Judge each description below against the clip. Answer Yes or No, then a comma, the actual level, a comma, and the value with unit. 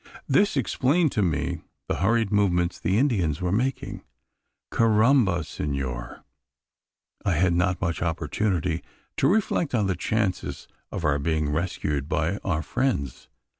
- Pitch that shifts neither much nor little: No, wide, 6.1 semitones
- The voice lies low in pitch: Yes, very low, 90 Hz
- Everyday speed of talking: No, slow, 130 wpm